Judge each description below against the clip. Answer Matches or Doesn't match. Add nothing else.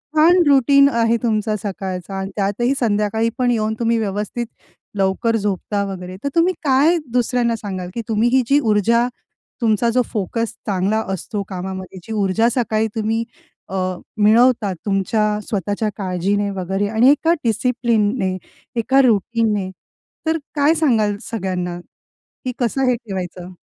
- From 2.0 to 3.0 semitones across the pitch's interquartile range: Doesn't match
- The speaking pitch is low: Doesn't match